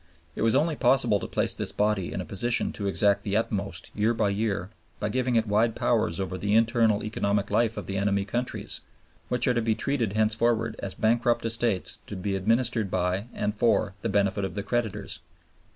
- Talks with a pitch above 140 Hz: No, low, 110 Hz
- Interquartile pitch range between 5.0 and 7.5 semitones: No, average, 2.7 semitones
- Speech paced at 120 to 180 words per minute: No, average, 200 wpm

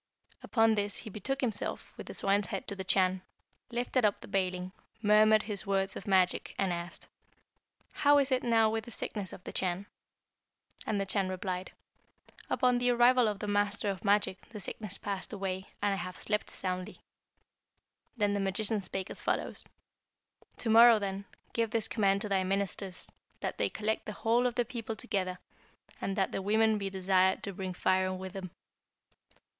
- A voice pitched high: Yes, high, 200 Hz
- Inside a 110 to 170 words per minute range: No, average, 180 wpm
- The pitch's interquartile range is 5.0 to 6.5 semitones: No, narrow, 2.6 semitones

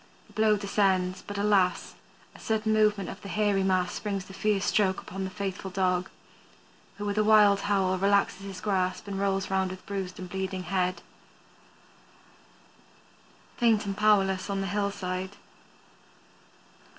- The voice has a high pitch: Yes, high, 195 Hz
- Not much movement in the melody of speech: Yes, narrow, 1.6 semitones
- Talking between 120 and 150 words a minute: Yes, average, 145 wpm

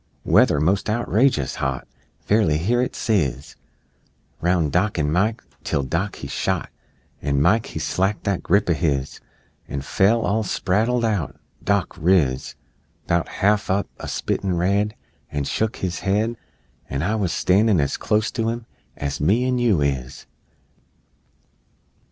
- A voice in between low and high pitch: No, very low, 95 Hz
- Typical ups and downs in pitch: No, wide, 6.1 semitones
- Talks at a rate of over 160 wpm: No, average, 150 wpm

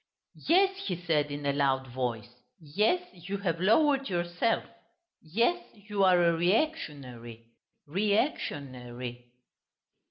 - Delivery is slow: Yes, slow, 125 wpm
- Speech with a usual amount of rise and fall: No, wide, 8.0 semitones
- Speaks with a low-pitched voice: No, medium, 170 Hz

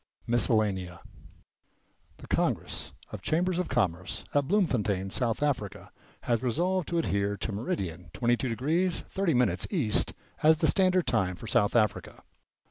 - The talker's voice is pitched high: No, low, 120 Hz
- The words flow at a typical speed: No, slow, 130 wpm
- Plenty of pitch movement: Yes, wide, 8.5 semitones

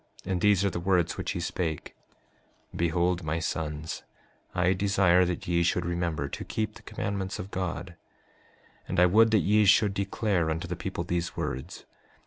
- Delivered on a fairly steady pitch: Yes, narrow, 2.3 semitones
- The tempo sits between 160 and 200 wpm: Yes, average, 175 wpm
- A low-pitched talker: Yes, very low, 90 Hz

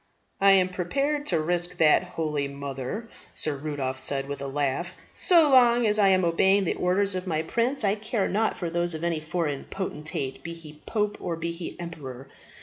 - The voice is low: No, medium, 175 Hz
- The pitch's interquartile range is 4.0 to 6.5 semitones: Yes, average, 4.7 semitones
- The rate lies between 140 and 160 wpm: No, average, 195 wpm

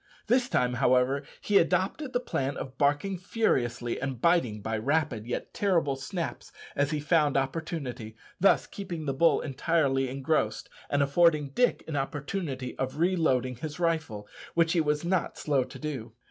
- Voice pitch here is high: No, medium, 145 Hz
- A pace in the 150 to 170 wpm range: Yes, average, 160 wpm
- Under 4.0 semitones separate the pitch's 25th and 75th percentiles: No, average, 4.4 semitones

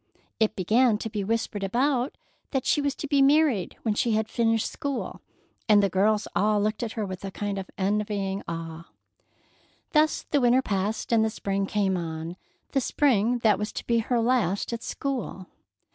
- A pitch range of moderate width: Yes, average, 3.8 semitones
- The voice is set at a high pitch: Yes, high, 215 Hz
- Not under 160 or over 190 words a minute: Yes, average, 185 wpm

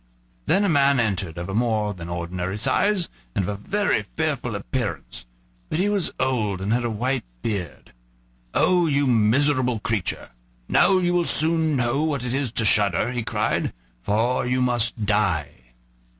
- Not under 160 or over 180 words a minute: Yes, average, 165 wpm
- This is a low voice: Yes, low, 120 Hz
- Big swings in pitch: Yes, wide, 5.7 semitones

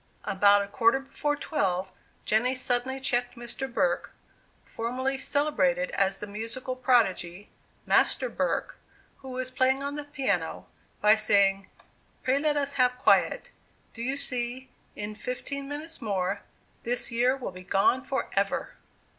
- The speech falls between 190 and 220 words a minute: No, average, 140 wpm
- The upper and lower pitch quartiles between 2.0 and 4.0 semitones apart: No, average, 4.6 semitones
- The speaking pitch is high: Yes, high, 245 Hz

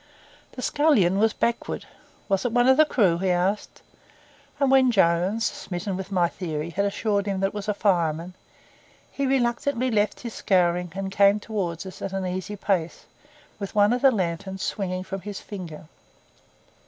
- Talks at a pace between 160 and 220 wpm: Yes, average, 175 wpm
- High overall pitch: Yes, high, 195 Hz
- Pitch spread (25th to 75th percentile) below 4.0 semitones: Yes, average, 3.4 semitones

